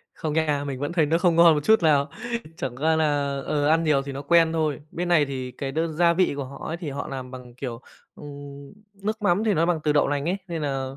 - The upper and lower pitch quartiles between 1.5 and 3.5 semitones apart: Yes, average, 3.0 semitones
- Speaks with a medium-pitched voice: Yes, medium, 150 Hz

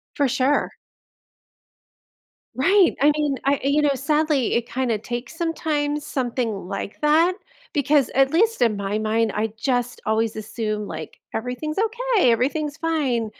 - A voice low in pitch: No, very high, 270 Hz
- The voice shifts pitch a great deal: No, average, 4.9 semitones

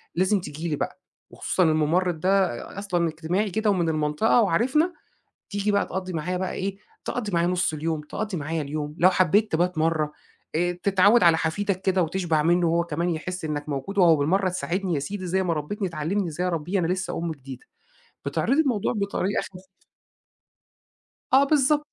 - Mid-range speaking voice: Yes, medium, 180 Hz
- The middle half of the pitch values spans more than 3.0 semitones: Yes, average, 3.7 semitones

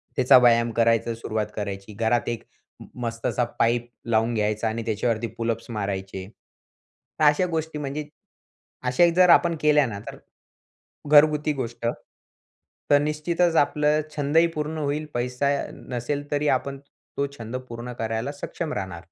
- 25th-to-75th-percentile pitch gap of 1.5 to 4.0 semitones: No, average, 4.6 semitones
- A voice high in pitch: No, low, 125 Hz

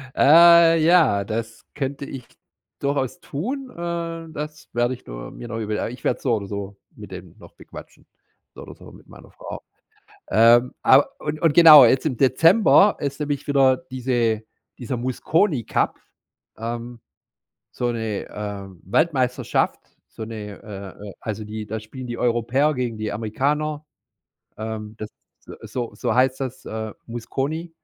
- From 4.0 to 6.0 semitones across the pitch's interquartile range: Yes, average, 5.2 semitones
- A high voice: No, low, 125 Hz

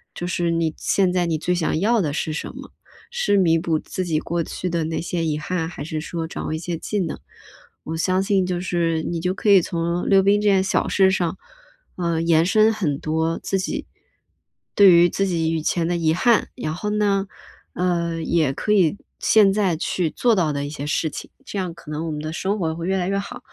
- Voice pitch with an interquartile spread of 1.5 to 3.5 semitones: Yes, average, 3.0 semitones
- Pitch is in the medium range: Yes, medium, 175 Hz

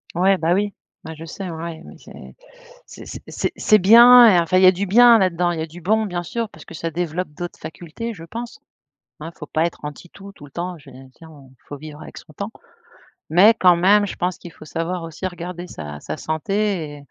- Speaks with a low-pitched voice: No, medium, 175 Hz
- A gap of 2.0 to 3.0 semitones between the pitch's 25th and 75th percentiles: No, average, 3.6 semitones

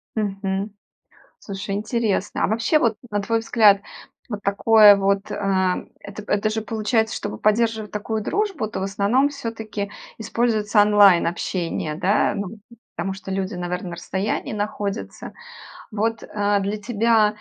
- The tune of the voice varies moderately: No, narrow, 2.0 semitones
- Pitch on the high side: Yes, high, 210 Hz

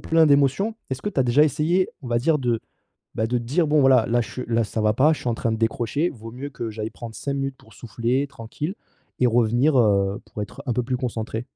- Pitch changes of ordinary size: Yes, average, 3.8 semitones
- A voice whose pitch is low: Yes, low, 125 Hz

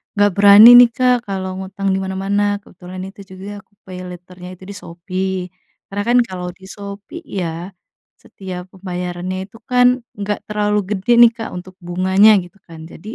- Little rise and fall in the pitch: Yes, narrow, 1.9 semitones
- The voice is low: No, high, 190 Hz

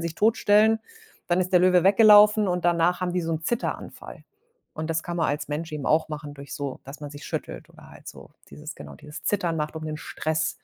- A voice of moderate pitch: Yes, medium, 165 Hz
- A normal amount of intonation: Yes, average, 3.3 semitones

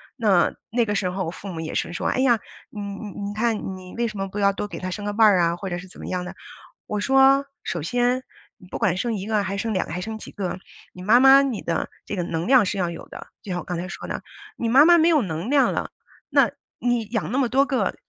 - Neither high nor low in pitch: No, high, 205 Hz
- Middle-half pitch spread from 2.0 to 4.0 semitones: No, average, 4.8 semitones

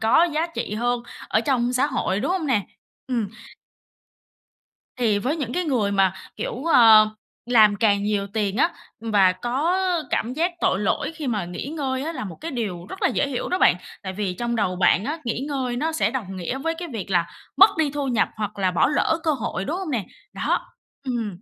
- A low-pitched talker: No, high, 240 Hz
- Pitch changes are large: Yes, wide, 6.1 semitones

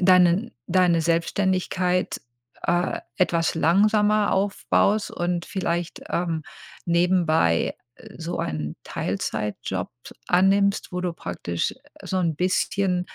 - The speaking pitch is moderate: Yes, medium, 180 Hz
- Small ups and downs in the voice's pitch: Yes, narrow, 2.1 semitones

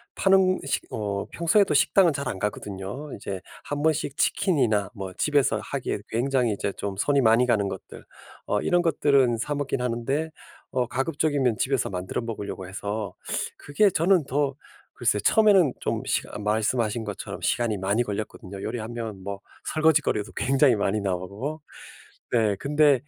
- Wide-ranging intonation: Yes, wide, 5.9 semitones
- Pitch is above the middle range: No, low, 120 Hz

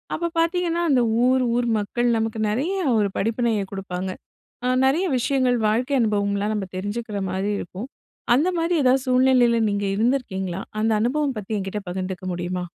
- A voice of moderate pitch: No, high, 225 Hz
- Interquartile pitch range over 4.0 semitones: Yes, average, 4.5 semitones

